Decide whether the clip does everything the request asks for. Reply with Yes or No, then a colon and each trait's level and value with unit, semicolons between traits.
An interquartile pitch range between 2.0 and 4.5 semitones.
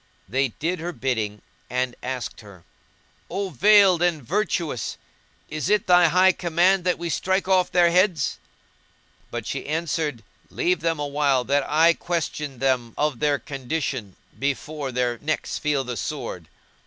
No: average, 5.1 semitones